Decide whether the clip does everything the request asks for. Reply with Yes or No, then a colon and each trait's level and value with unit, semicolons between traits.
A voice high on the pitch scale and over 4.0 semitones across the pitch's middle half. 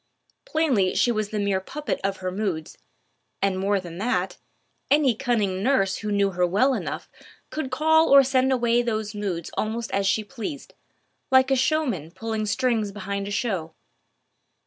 Yes: high, 215 Hz; average, 4.8 semitones